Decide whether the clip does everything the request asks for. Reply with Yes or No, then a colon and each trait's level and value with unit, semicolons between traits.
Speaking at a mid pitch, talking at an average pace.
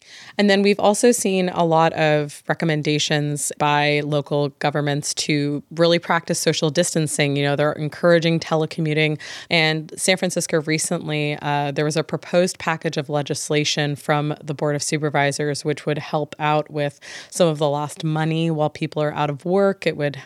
Yes: medium, 155 Hz; average, 170 wpm